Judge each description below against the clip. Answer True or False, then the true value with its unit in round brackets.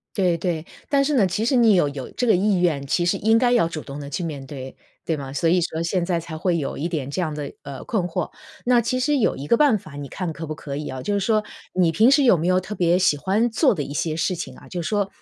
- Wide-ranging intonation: True (5.8 semitones)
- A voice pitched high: False (175 Hz)